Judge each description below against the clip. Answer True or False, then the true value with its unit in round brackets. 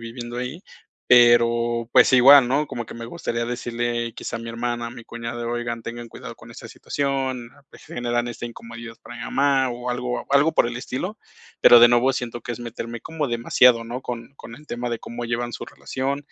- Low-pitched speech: True (120 Hz)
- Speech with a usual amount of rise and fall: False (1.4 semitones)